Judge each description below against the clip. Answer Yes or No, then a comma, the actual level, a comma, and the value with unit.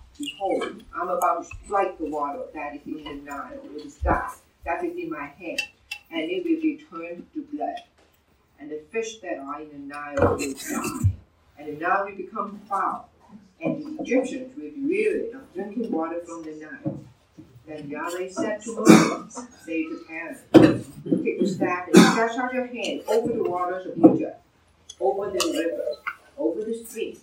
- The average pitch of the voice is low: No, high, 200 Hz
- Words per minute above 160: Yes, average, 185 wpm